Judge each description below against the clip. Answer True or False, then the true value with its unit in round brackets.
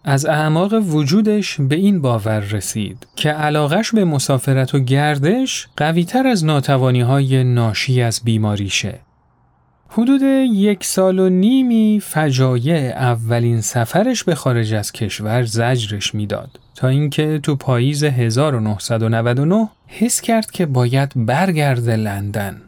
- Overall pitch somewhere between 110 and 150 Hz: True (140 Hz)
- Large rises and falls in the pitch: True (7.6 semitones)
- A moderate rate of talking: True (120 wpm)